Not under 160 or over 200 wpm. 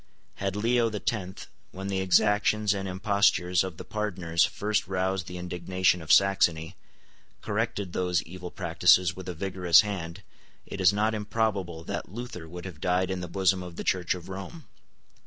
Yes: average, 170 wpm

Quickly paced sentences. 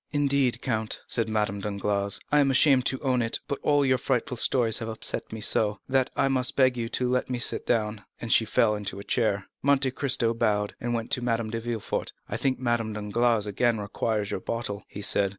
Yes: fast, 215 wpm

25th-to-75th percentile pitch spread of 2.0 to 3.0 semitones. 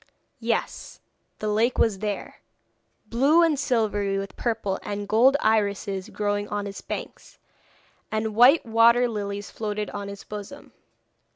Yes: narrow, 2.4 semitones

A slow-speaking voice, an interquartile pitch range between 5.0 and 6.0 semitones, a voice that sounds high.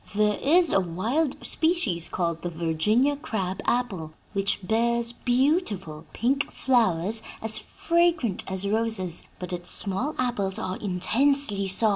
Yes: slow, 130 wpm; wide, 5.6 semitones; high, 215 Hz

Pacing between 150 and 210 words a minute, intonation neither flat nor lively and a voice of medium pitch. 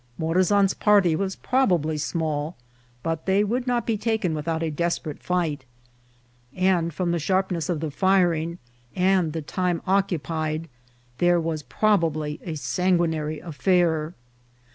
No: slow, 135 wpm; average, 3.1 semitones; medium, 170 Hz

